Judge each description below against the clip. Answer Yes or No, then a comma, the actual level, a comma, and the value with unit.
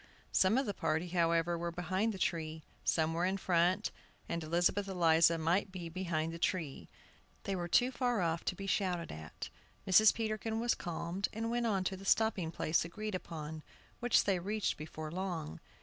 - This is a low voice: No, medium, 180 Hz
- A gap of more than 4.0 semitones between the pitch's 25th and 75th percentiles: No, average, 3.3 semitones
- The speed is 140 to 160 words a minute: No, average, 180 wpm